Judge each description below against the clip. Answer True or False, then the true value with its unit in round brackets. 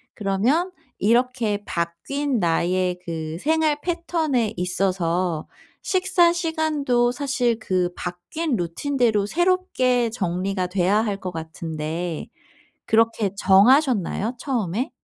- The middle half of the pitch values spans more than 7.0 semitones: True (7.5 semitones)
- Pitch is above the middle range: True (220 Hz)